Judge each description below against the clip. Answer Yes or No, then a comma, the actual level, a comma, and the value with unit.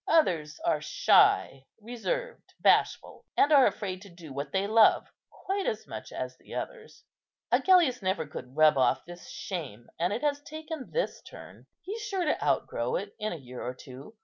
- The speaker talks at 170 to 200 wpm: Yes, average, 175 wpm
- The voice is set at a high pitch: Yes, high, 215 Hz